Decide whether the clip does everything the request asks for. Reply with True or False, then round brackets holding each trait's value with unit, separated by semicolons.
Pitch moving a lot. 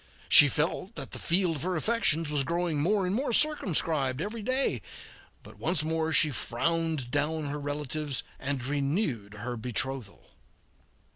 False (4.3 semitones)